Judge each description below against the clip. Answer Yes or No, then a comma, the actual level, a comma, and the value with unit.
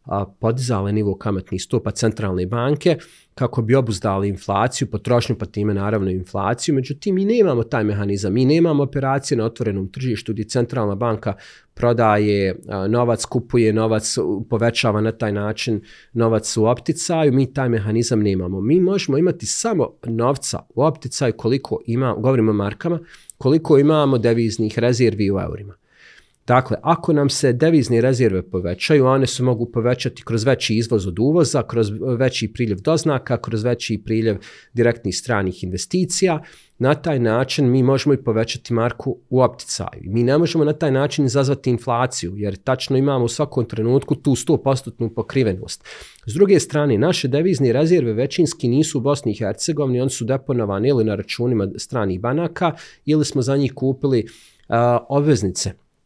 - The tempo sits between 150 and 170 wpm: Yes, average, 155 wpm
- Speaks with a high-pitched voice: No, low, 120 Hz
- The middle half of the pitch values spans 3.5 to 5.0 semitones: Yes, average, 4.3 semitones